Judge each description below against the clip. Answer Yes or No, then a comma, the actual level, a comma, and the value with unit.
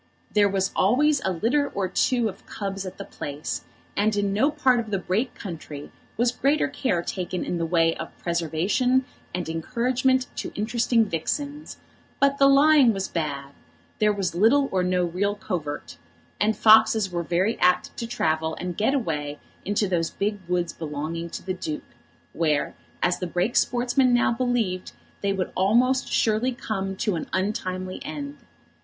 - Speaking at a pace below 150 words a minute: No, average, 165 wpm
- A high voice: Yes, high, 195 Hz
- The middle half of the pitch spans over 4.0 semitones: Yes, wide, 5.5 semitones